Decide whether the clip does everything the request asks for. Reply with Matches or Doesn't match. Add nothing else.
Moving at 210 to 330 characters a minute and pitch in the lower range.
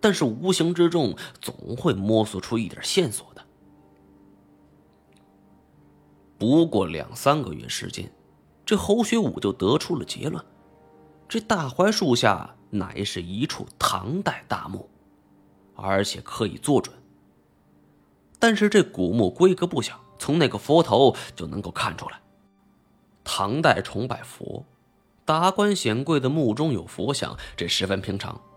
Doesn't match